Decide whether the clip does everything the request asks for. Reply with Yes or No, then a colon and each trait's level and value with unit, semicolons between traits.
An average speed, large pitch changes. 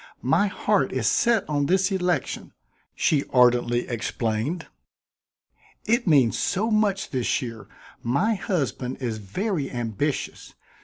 No: slow, 115 wpm; wide, 8.1 semitones